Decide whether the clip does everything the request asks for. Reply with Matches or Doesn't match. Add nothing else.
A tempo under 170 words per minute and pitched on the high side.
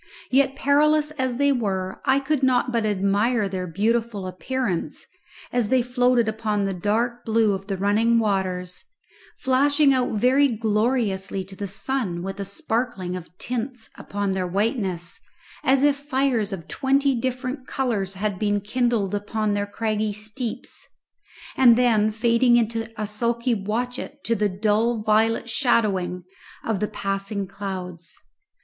Matches